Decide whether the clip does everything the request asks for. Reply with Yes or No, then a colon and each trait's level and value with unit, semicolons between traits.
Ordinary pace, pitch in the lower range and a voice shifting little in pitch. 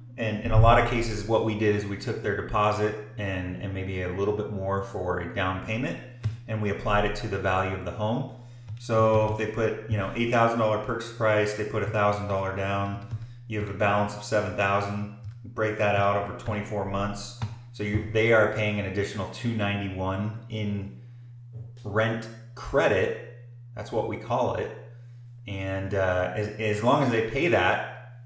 Yes: average, 180 wpm; low, 105 Hz; narrow, 2.3 semitones